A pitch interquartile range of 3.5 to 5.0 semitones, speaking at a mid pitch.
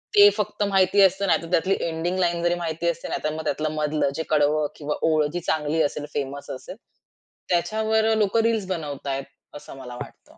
Yes: average, 4.2 semitones; medium, 165 Hz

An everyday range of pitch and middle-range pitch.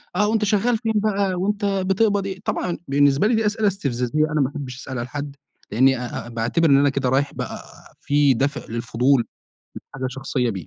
No: wide, 7.3 semitones; medium, 145 Hz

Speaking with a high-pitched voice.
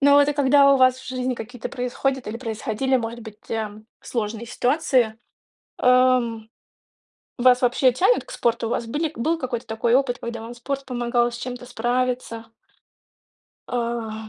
Yes: high, 245 Hz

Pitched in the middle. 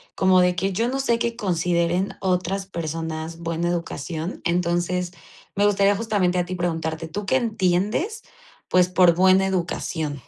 Yes: medium, 180 Hz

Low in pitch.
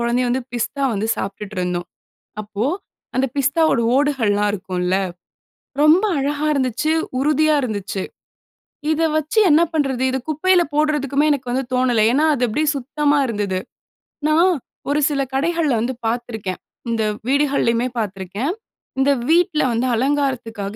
No: very high, 260 Hz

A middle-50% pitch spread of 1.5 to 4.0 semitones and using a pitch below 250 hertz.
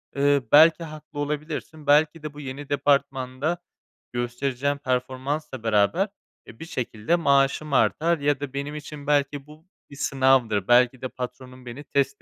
Yes: narrow, 2.6 semitones; medium, 140 Hz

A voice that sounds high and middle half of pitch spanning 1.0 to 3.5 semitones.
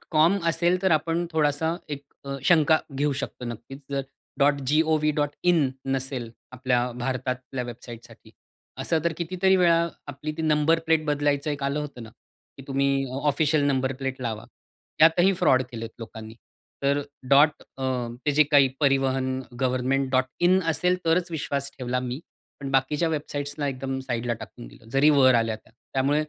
No: medium, 140 Hz; average, 3.1 semitones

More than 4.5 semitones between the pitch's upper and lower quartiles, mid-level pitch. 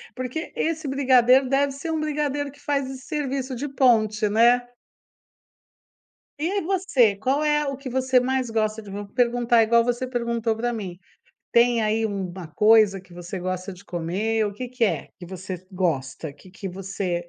No: average, 5.2 semitones; high, 235 Hz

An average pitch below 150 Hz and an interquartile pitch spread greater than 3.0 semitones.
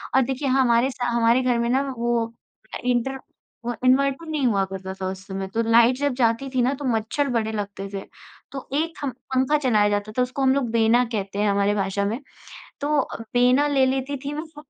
No: high, 245 Hz; average, 3.7 semitones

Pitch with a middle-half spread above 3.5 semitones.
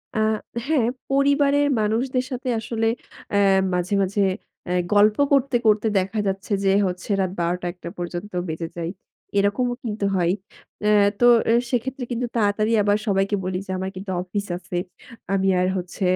Yes: average, 4.2 semitones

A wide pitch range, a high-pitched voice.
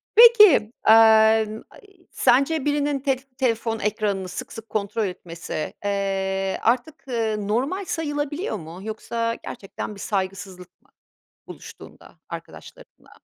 Yes: wide, 5.7 semitones; high, 220 Hz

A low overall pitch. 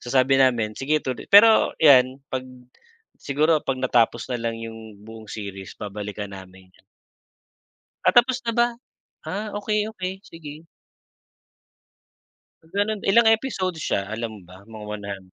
Yes: low, 130 Hz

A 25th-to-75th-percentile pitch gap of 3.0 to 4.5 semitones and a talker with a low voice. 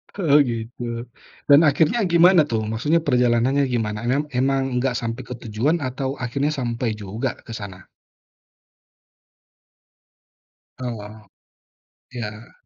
Yes: average, 3.6 semitones; low, 125 Hz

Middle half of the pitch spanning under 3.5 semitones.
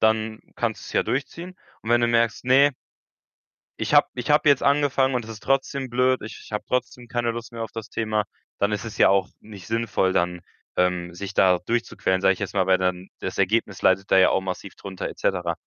No: average, 4.3 semitones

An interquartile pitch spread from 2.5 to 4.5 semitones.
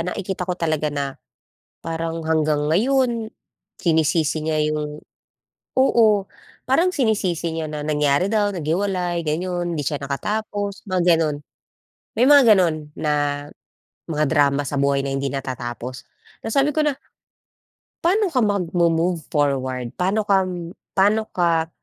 No: average, 5.2 semitones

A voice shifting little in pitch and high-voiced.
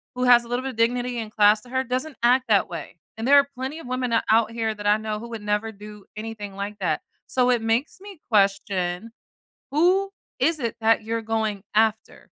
No: average, 3.1 semitones; high, 225 Hz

